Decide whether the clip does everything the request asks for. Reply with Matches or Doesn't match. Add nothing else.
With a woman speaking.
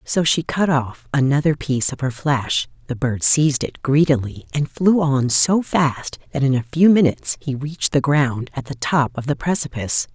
Matches